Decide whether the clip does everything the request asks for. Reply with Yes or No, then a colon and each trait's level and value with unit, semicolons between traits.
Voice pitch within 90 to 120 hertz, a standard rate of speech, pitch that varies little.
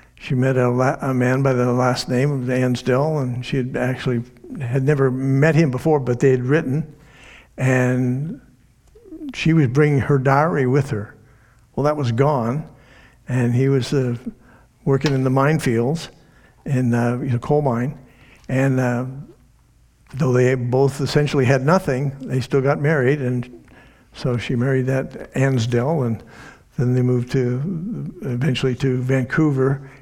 No: low, 130 Hz; average, 150 wpm; narrow, 2.2 semitones